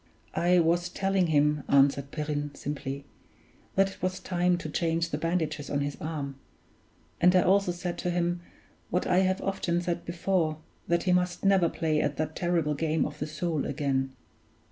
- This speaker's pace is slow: No, average, 175 wpm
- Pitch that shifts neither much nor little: Yes, average, 3.1 semitones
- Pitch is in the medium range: Yes, medium, 165 Hz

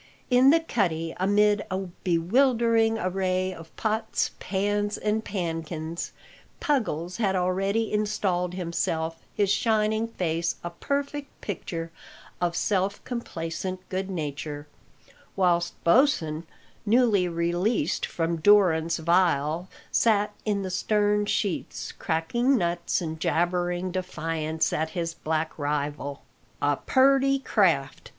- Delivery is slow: Yes, slow, 110 wpm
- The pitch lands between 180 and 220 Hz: Yes, medium, 185 Hz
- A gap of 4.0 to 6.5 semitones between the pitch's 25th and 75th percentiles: Yes, average, 4.3 semitones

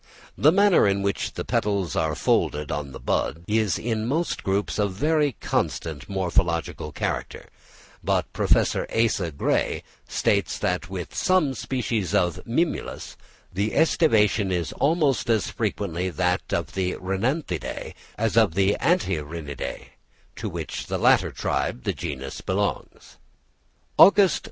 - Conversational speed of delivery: No, slow, 130 wpm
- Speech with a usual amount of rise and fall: No, wide, 6.5 semitones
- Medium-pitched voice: No, low, 100 Hz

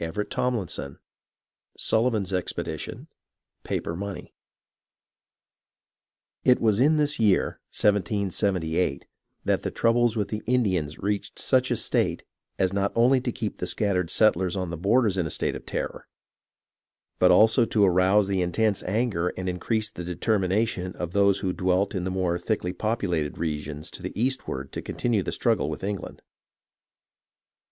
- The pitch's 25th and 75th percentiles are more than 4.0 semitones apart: No, average, 3.6 semitones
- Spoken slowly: No, average, 150 wpm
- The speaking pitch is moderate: No, low, 100 Hz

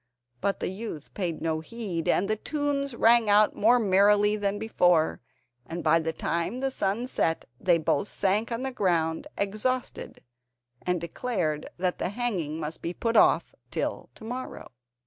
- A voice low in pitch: No, high, 200 Hz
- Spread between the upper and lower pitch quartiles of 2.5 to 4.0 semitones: No, wide, 5.5 semitones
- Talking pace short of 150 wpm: No, average, 165 wpm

